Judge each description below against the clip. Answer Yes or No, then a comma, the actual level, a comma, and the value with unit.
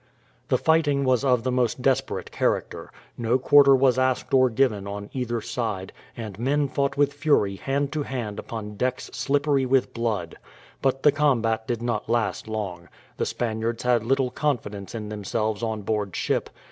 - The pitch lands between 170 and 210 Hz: No, low, 120 Hz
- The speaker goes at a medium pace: Yes, average, 170 wpm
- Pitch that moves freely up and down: No, average, 3.7 semitones